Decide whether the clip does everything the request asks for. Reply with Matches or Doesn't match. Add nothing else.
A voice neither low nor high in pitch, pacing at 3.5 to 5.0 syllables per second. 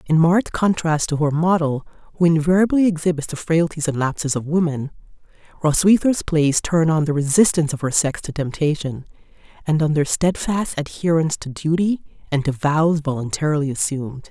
Doesn't match